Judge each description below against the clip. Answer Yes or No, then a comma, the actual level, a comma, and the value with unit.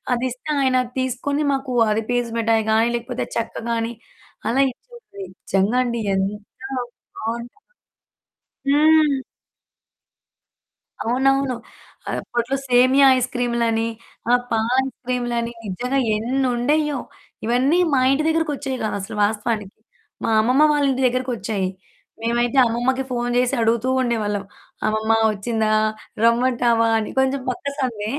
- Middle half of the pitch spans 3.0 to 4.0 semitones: No, narrow, 2.6 semitones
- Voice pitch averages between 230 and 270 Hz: Yes, high, 245 Hz